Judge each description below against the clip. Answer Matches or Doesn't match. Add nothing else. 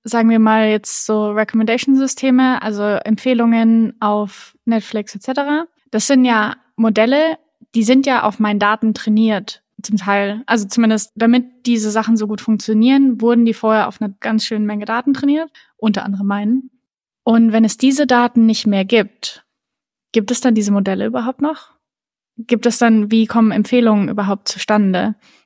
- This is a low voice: Doesn't match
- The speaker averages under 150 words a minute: Doesn't match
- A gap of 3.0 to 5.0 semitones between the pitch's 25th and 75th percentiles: Doesn't match